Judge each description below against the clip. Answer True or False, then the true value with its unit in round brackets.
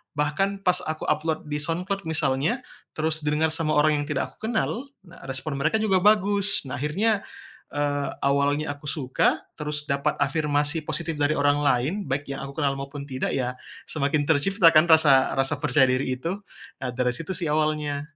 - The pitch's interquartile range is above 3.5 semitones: False (2.7 semitones)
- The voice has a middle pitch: True (150 Hz)